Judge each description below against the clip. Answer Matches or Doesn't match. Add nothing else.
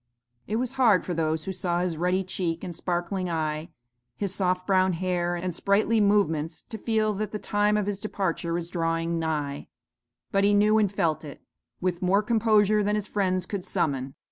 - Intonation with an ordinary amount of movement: Matches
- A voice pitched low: Doesn't match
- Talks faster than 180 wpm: Matches